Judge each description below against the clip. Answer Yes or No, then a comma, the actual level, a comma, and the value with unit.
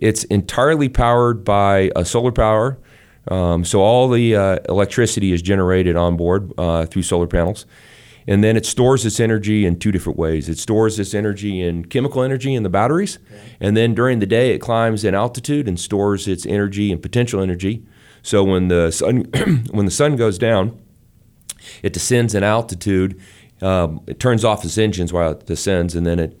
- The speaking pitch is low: Yes, low, 105 Hz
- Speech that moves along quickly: No, average, 185 wpm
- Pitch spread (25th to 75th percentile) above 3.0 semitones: Yes, average, 3.8 semitones